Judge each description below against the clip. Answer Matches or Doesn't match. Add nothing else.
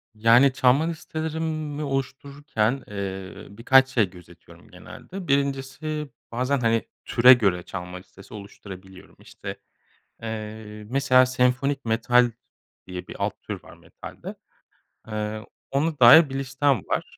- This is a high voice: Doesn't match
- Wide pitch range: Doesn't match